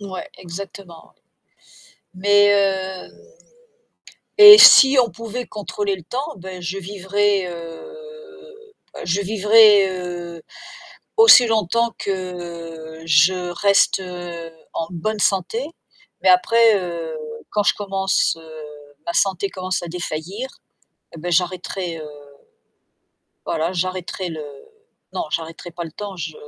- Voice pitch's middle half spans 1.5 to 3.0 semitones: No, average, 3.6 semitones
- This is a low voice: No, high, 190 Hz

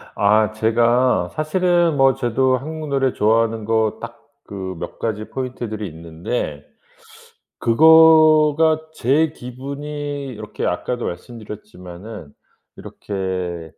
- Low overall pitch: Yes, low, 120 Hz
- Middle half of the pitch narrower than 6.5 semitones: Yes, wide, 5.4 semitones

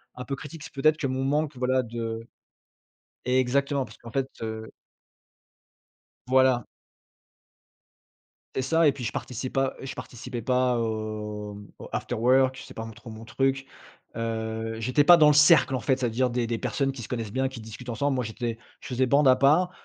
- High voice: No, low, 125 Hz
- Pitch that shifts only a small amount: No, average, 3.0 semitones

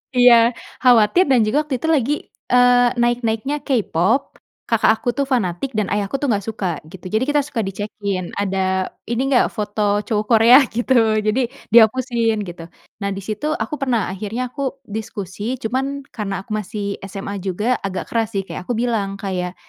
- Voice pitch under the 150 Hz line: No, high, 220 Hz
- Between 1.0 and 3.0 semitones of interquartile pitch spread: No, average, 3.7 semitones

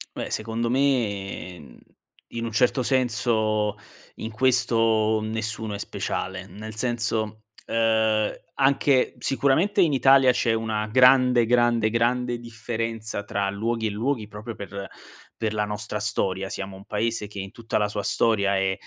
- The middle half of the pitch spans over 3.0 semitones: No, narrow, 2.4 semitones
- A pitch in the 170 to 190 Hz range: No, low, 110 Hz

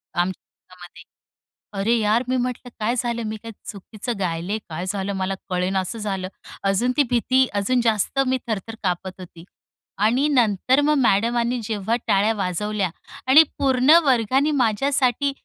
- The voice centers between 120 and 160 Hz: No, high, 220 Hz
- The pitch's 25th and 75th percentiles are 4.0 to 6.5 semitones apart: Yes, average, 4.5 semitones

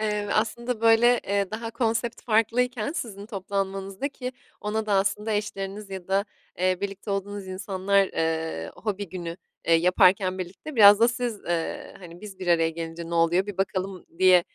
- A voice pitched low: No, high, 195 Hz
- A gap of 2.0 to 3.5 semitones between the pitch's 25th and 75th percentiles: Yes, average, 2.9 semitones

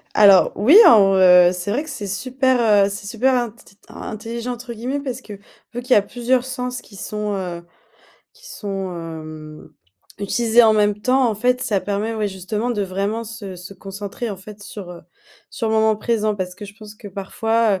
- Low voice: No, high, 210 Hz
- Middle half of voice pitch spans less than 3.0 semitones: No, average, 3.3 semitones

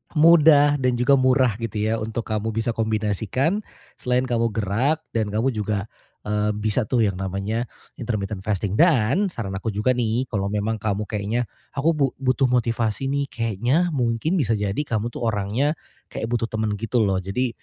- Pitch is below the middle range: Yes, low, 115 Hz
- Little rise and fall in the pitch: No, average, 3.4 semitones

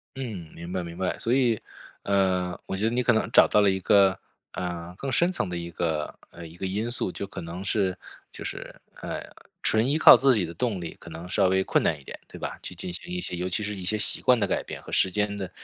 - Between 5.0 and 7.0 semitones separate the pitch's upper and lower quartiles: No, average, 3.8 semitones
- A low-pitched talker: Yes, very low, 95 Hz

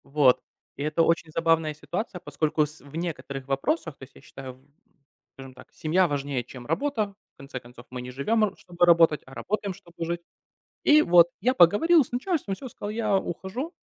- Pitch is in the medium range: Yes, medium, 165 Hz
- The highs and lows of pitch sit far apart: Yes, wide, 6.7 semitones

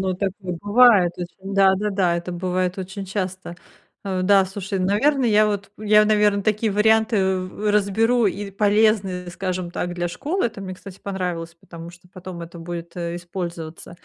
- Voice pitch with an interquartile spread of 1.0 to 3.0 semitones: Yes, average, 2.7 semitones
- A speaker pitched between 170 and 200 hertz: Yes, high, 190 Hz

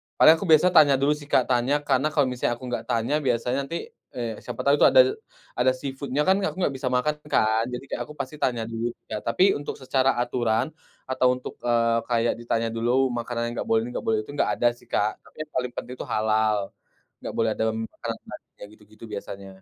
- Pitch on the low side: Yes, low, 125 Hz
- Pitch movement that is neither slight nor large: Yes, average, 3.2 semitones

